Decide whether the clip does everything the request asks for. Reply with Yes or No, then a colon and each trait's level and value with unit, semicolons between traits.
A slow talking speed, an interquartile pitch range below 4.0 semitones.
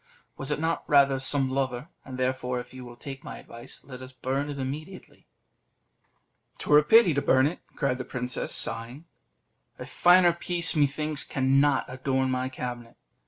No: average, 165 wpm; narrow, 2.5 semitones